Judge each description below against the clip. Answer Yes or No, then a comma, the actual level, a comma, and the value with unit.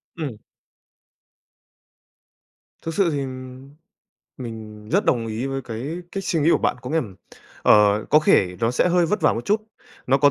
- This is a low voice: Yes, low, 130 Hz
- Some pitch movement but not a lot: No, wide, 6.2 semitones